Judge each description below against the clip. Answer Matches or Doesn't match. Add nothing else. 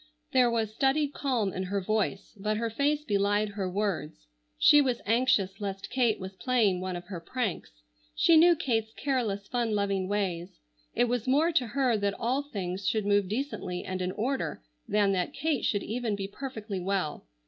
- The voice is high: Matches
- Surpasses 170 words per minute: Matches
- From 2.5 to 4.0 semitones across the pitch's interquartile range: Doesn't match